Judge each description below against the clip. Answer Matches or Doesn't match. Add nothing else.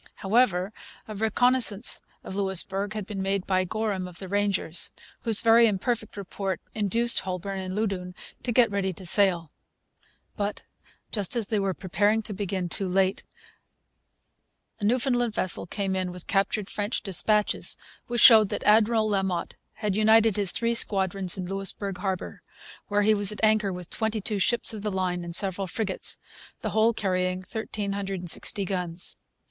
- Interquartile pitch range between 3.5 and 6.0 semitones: Doesn't match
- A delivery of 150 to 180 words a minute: Matches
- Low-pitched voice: Doesn't match